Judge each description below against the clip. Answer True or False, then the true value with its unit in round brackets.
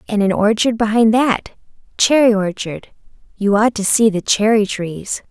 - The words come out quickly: False (145 wpm)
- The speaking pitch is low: False (215 Hz)